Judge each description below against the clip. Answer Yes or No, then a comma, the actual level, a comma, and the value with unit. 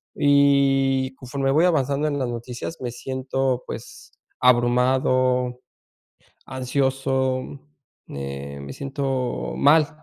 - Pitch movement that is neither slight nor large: No, narrow, 1.7 semitones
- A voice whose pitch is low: Yes, low, 130 Hz